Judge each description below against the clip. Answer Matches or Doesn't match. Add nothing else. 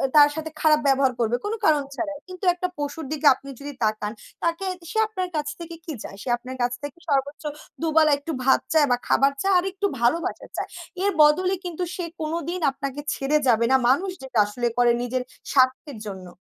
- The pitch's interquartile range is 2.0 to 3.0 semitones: Doesn't match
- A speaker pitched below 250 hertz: Doesn't match